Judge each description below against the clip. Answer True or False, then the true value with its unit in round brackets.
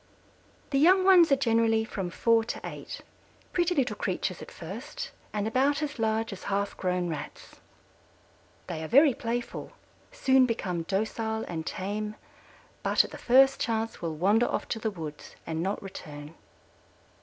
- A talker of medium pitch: False (220 Hz)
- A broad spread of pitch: True (5.8 semitones)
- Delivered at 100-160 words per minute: True (155 wpm)